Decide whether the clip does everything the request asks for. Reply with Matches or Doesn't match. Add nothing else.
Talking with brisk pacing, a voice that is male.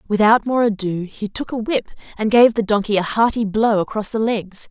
Doesn't match